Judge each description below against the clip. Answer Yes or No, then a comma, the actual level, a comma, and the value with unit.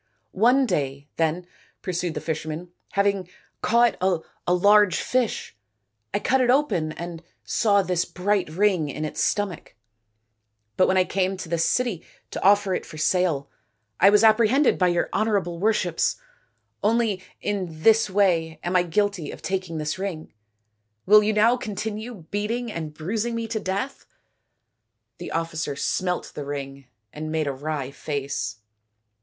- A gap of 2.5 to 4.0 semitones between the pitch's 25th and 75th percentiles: No, average, 4.7 semitones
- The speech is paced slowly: No, average, 160 wpm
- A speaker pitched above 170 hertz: Yes, medium, 185 Hz